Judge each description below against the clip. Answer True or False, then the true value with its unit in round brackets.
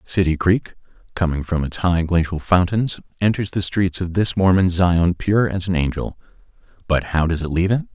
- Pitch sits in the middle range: False (90 Hz)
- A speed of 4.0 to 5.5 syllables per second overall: True (5.1 syllables/s)